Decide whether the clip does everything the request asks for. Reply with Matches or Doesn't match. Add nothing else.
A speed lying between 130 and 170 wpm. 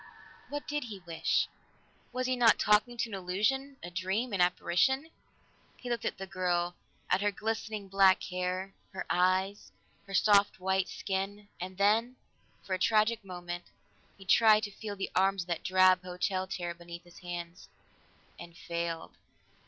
Matches